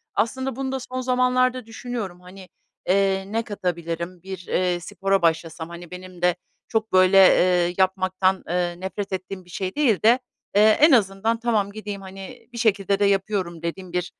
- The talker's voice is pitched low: No, high, 195 Hz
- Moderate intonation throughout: Yes, average, 3.6 semitones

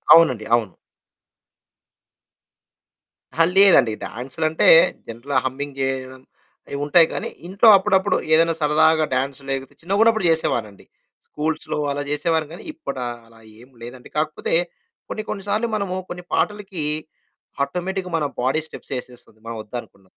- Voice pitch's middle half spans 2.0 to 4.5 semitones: No, wide, 5.6 semitones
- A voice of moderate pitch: Yes, medium, 150 Hz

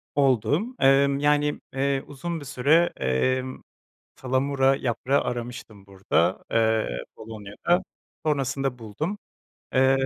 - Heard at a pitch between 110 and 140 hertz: Yes, low, 135 Hz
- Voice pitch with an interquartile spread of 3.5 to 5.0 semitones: Yes, average, 3.8 semitones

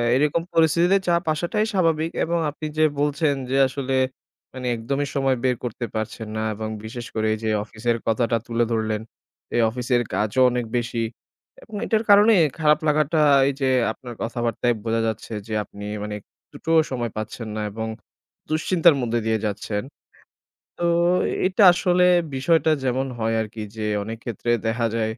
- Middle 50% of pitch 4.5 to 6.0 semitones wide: Yes, wide, 5.6 semitones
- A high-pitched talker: No, low, 125 Hz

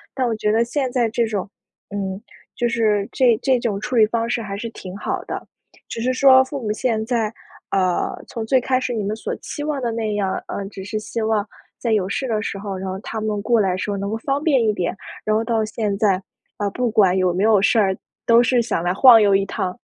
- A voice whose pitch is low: No, high, 220 Hz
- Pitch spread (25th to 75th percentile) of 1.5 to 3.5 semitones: Yes, average, 3.0 semitones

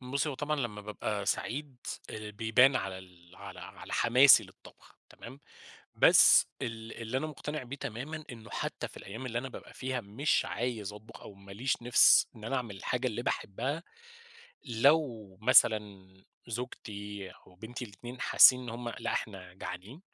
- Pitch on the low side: Yes, low, 115 Hz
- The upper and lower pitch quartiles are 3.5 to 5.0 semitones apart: Yes, average, 3.9 semitones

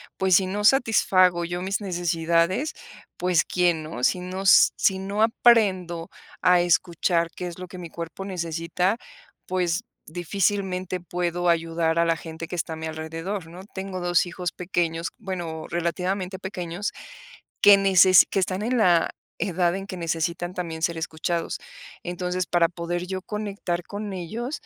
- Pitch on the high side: No, medium, 180 Hz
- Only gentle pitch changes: Yes, narrow, 2.1 semitones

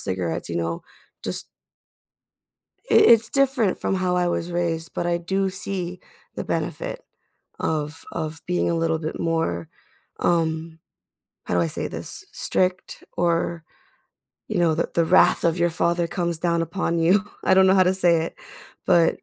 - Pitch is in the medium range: Yes, medium, 170 Hz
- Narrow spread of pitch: Yes, narrow, 2.2 semitones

